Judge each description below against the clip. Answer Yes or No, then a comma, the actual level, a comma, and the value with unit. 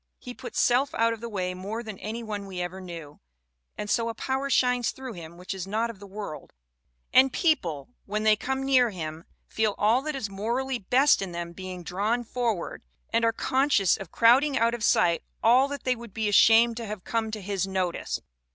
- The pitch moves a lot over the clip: No, average, 4.3 semitones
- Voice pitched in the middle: No, high, 220 Hz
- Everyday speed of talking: No, fast, 210 wpm